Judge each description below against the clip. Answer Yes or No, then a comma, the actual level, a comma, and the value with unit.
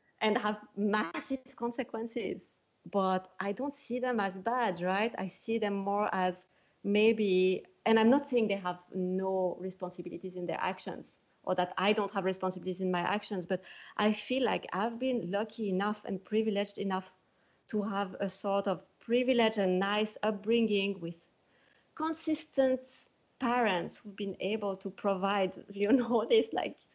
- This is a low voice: No, high, 205 Hz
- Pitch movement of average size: Yes, average, 3.4 semitones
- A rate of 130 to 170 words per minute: Yes, average, 155 wpm